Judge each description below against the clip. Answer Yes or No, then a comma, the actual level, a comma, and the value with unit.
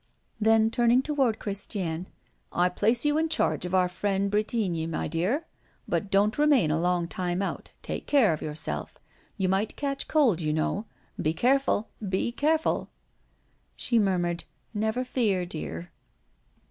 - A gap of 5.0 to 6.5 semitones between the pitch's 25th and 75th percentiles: Yes, wide, 5.4 semitones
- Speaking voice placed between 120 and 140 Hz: No, high, 205 Hz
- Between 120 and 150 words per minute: Yes, average, 145 wpm